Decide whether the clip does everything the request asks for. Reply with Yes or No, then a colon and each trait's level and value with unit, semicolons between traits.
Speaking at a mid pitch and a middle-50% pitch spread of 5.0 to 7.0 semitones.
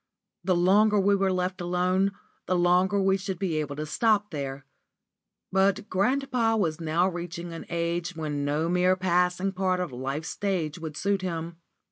No: medium, 180 Hz; average, 2.8 semitones